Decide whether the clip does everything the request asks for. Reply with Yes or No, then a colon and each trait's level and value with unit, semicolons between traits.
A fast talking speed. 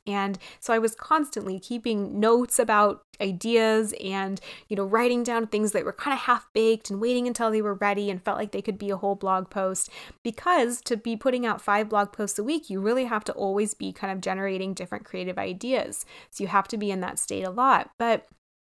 Yes: fast, 225 wpm